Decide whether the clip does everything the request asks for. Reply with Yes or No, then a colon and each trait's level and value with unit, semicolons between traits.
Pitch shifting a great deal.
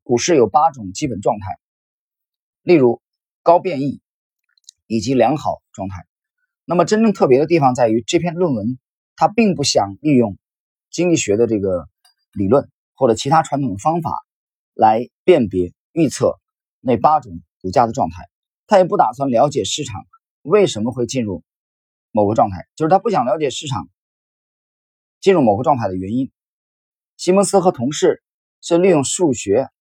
Yes: wide, 7.7 semitones